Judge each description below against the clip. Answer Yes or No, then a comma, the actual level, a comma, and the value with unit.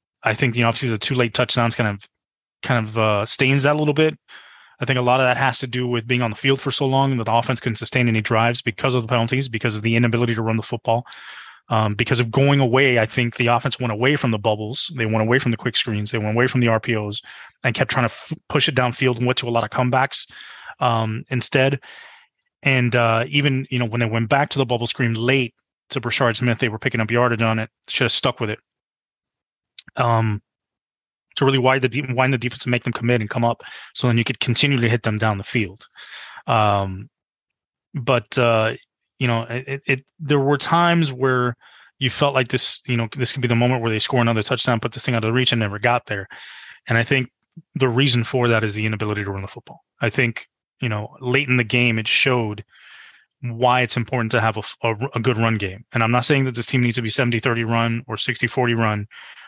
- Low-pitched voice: Yes, low, 120 Hz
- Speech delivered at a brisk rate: Yes, fast, 245 wpm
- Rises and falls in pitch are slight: Yes, narrow, 2.3 semitones